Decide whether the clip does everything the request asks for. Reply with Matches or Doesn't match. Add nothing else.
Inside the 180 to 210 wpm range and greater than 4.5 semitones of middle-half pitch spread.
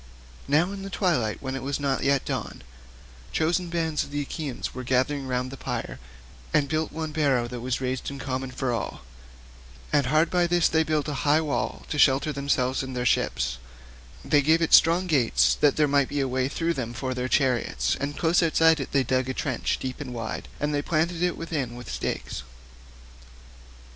Doesn't match